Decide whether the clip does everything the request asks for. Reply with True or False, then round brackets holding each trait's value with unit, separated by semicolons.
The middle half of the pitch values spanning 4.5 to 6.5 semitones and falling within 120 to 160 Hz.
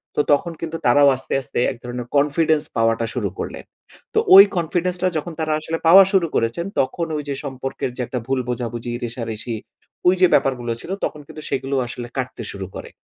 True (5.0 semitones; 135 Hz)